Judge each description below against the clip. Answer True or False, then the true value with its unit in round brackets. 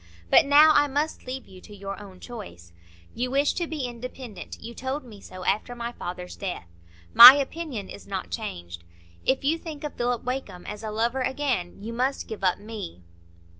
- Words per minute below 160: False (190 wpm)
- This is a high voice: True (235 Hz)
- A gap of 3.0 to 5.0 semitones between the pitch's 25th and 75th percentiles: False (5.4 semitones)